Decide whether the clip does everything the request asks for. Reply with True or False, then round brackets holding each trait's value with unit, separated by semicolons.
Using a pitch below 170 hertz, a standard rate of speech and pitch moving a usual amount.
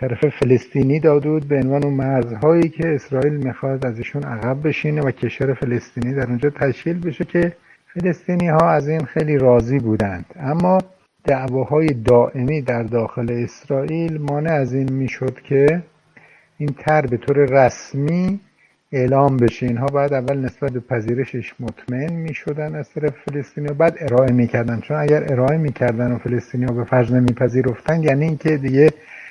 True (140 Hz; 145 wpm; 3.4 semitones)